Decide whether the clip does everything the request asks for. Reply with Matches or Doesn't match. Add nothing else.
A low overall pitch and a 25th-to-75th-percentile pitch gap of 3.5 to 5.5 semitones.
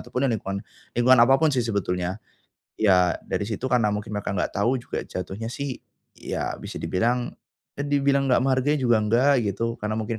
Matches